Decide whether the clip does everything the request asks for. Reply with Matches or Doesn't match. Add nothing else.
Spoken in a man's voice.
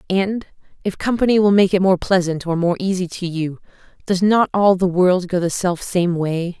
Doesn't match